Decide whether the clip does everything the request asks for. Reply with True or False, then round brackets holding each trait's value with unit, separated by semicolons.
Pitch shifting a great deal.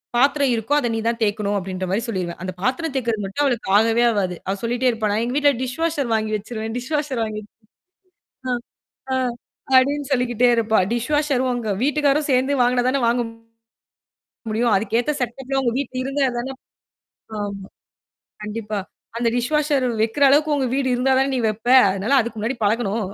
False (3.8 semitones)